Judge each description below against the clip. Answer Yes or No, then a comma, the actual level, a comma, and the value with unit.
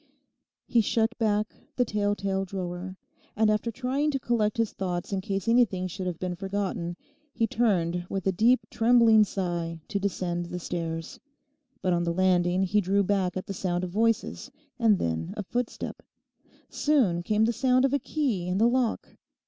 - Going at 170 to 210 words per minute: Yes, average, 180 wpm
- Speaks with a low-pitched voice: No, high, 195 Hz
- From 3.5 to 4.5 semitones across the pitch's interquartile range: Yes, average, 4.2 semitones